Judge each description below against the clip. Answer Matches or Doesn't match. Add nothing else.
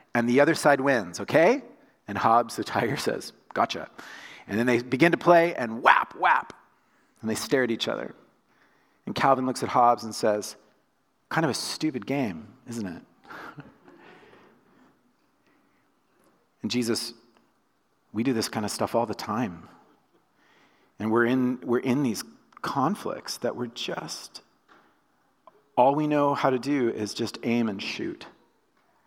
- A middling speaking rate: Matches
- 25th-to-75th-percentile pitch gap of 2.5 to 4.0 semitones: Matches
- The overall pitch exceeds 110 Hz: Matches